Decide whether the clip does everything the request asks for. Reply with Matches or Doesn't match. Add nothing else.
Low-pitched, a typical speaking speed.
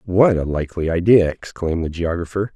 Matches